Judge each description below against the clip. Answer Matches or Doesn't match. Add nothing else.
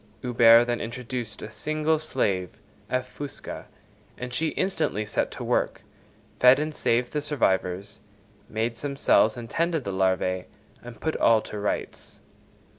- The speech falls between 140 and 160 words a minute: Matches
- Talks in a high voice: Doesn't match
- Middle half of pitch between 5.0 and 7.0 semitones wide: Matches